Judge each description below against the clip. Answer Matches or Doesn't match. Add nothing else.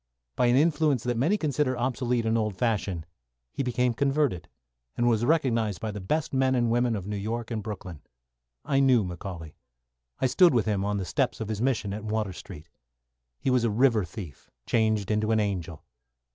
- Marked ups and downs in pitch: Doesn't match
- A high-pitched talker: Doesn't match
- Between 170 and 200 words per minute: Matches